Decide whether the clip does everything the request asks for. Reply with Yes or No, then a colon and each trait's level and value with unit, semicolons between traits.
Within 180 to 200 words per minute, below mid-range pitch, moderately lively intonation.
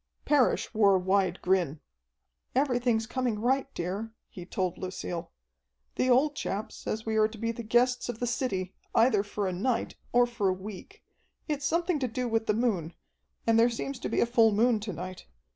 No: average, 195 wpm; high, 225 Hz; average, 4.2 semitones